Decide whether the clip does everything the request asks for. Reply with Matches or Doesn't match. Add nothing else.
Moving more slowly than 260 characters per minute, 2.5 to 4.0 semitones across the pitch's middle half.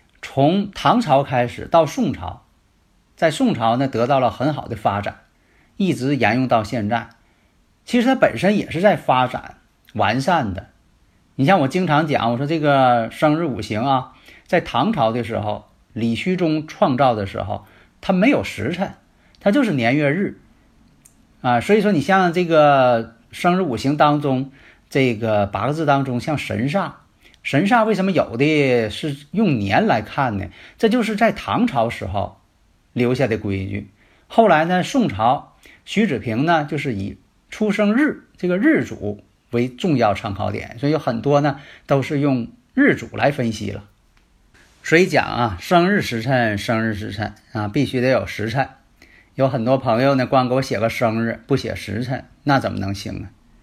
Doesn't match